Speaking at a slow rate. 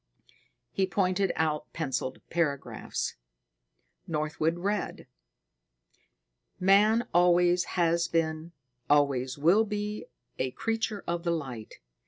Yes: slow, 95 wpm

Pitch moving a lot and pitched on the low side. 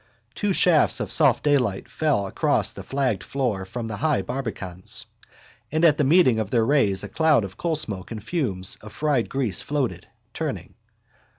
Yes: wide, 6.2 semitones; low, 125 Hz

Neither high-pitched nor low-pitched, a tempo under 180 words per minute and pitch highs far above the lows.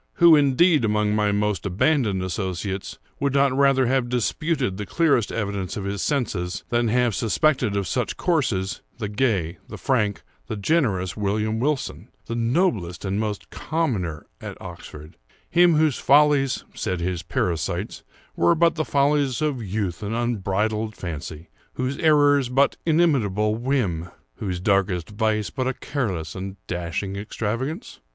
No: low, 110 Hz; average, 140 wpm; wide, 6.3 semitones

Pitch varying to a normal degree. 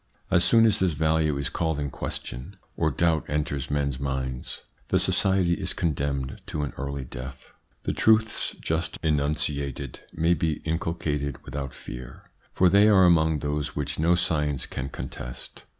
Yes: average, 3.2 semitones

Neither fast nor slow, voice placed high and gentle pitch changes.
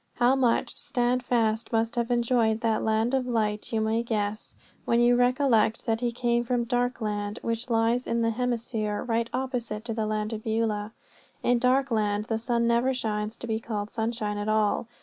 Yes: average, 180 wpm; high, 230 Hz; narrow, 1.9 semitones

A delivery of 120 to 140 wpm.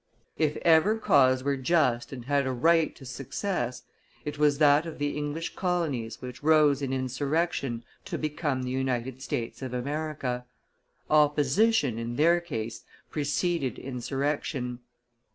Yes: slow, 135 wpm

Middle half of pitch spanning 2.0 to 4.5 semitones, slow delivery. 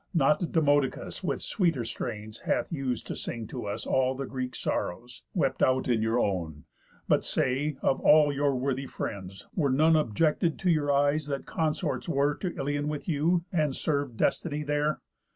No: average, 3.2 semitones; average, 170 wpm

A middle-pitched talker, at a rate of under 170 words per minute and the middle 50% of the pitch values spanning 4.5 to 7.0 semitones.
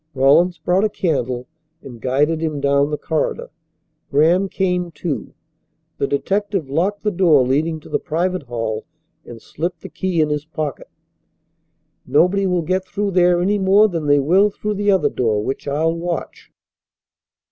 Yes: medium, 165 Hz; average, 160 wpm; average, 4.8 semitones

